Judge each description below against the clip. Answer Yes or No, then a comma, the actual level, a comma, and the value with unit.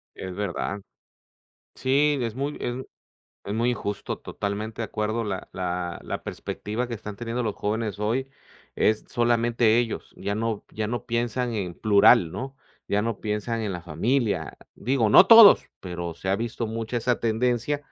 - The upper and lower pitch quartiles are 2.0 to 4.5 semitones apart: Yes, average, 2.9 semitones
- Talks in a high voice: No, low, 110 Hz